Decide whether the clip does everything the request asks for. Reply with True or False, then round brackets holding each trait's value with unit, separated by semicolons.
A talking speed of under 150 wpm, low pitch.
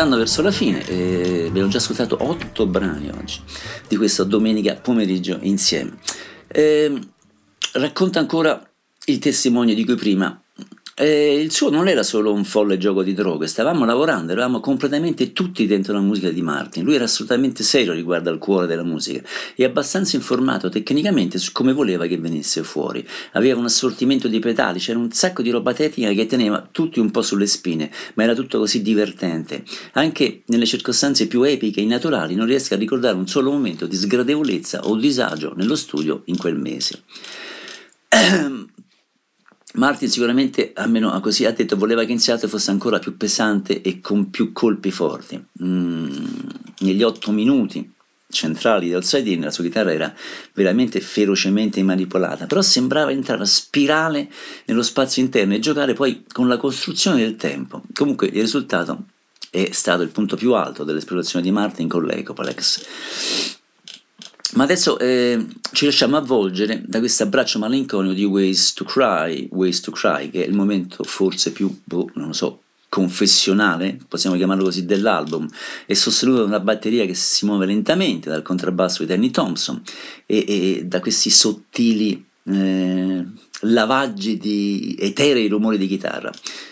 False (160 wpm; 110 Hz)